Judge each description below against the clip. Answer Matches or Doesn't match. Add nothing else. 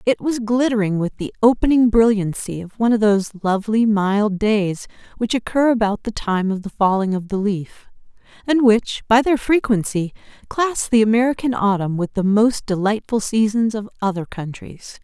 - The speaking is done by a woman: Matches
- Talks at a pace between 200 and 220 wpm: Doesn't match